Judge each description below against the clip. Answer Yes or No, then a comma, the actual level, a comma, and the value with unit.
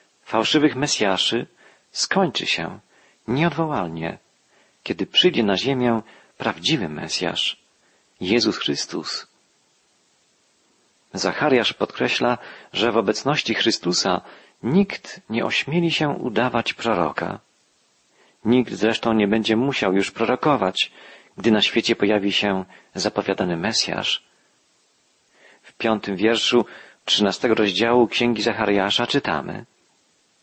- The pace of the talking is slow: Yes, slow, 95 wpm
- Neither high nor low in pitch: No, low, 115 Hz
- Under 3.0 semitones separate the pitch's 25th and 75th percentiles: No, average, 3.3 semitones